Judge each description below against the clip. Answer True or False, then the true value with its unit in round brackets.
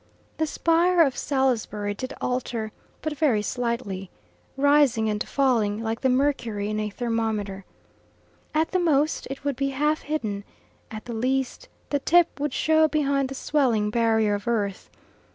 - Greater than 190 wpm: False (150 wpm)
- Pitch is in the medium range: False (255 Hz)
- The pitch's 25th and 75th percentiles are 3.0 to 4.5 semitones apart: False (5.0 semitones)